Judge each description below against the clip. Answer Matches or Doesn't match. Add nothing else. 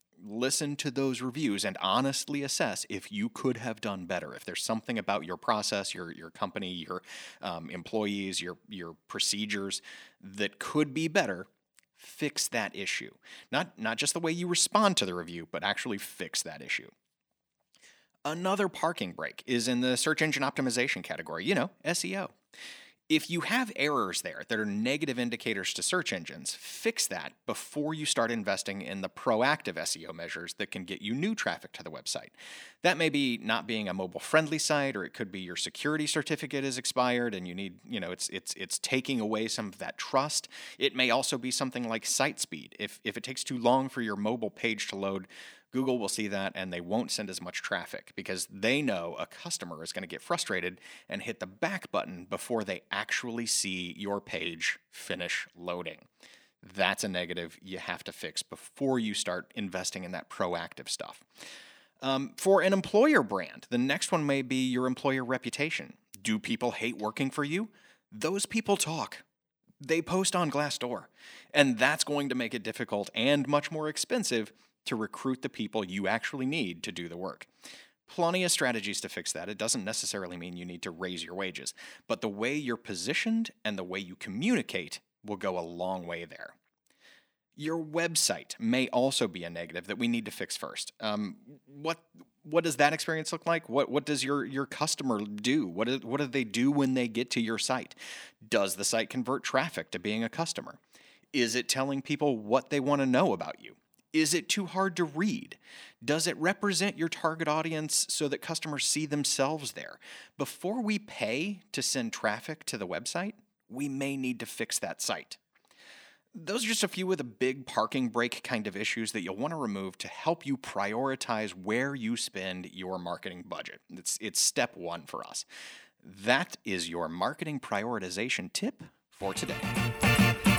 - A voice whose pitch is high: Doesn't match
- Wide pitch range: Matches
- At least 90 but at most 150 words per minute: Doesn't match